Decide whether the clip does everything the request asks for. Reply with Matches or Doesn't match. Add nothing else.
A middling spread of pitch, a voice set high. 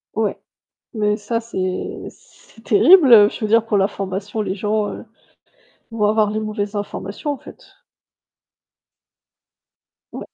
Doesn't match